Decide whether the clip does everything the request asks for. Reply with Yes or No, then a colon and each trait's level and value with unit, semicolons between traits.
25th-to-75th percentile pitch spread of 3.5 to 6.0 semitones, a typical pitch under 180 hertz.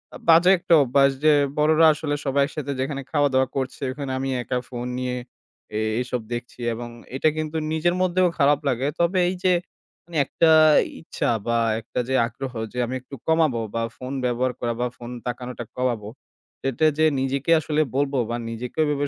Yes: average, 3.8 semitones; low, 135 Hz